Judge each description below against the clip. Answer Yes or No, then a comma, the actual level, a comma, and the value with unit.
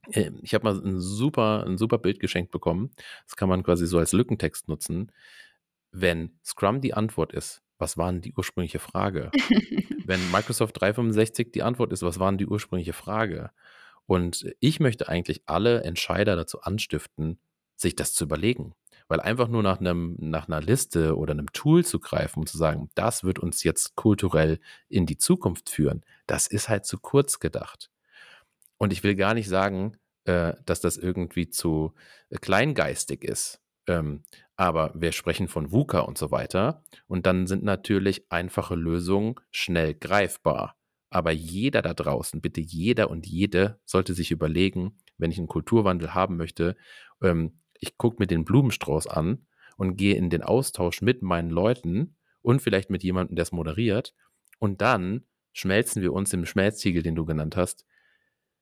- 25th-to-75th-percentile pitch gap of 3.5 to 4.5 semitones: Yes, average, 4.0 semitones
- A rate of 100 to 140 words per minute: No, average, 165 wpm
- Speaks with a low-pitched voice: Yes, very low, 95 Hz